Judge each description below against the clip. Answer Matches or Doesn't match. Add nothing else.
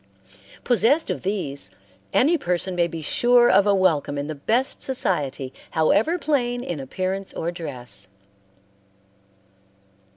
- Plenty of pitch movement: Matches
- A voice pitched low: Doesn't match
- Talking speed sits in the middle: Doesn't match